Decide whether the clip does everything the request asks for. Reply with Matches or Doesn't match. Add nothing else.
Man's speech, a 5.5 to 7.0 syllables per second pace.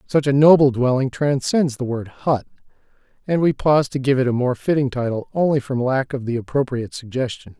Matches